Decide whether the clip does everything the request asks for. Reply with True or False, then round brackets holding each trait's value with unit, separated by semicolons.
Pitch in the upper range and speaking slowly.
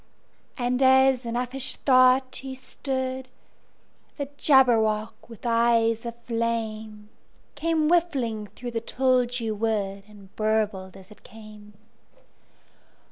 True (235 Hz; 95 wpm)